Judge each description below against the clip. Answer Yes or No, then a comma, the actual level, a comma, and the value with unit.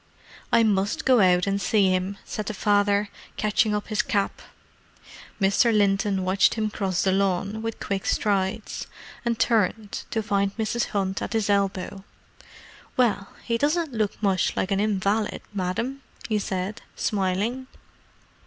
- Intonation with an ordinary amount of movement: No, narrow, 2.2 semitones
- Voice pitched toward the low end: No, high, 205 Hz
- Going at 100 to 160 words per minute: Yes, average, 145 wpm